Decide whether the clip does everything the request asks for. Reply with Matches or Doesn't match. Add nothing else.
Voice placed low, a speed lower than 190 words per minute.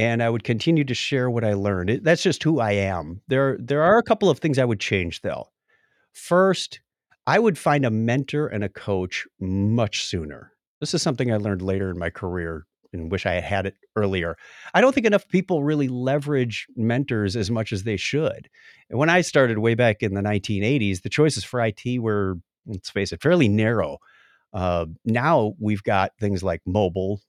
Doesn't match